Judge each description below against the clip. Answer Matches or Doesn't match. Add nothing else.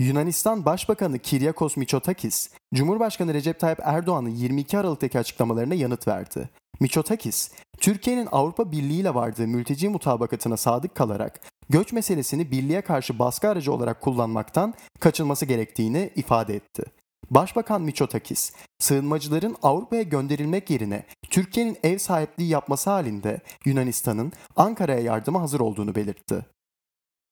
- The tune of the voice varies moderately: Doesn't match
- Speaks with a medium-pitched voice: Matches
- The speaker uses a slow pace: Doesn't match